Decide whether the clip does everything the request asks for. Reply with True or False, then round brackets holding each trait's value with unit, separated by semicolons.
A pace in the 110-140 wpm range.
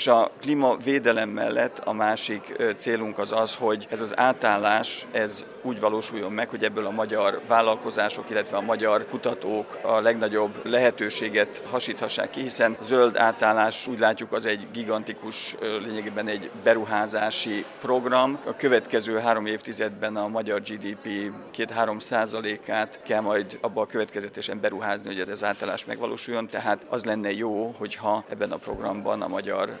False (150 wpm)